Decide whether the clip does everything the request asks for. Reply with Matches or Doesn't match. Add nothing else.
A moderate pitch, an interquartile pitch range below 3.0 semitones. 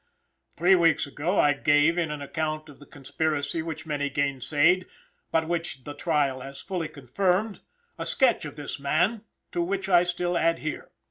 Doesn't match